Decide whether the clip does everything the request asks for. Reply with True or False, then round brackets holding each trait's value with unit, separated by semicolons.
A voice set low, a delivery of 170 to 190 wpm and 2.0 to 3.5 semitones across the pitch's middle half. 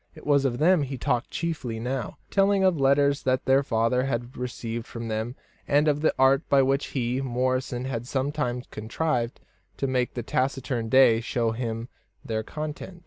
True (130 Hz; 175 wpm; 2.9 semitones)